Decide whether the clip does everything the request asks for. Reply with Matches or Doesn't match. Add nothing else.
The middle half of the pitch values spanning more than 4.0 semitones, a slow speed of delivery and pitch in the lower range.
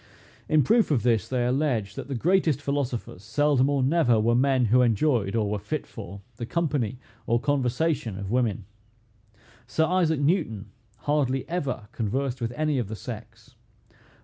Doesn't match